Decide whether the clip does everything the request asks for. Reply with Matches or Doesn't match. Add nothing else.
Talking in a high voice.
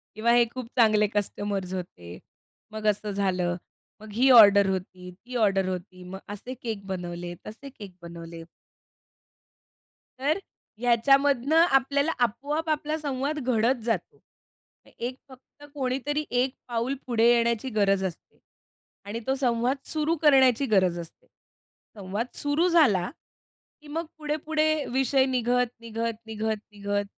Matches